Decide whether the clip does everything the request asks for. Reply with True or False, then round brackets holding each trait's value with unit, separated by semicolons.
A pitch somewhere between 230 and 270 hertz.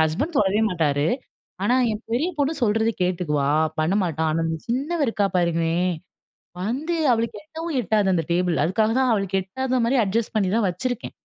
False (205 Hz)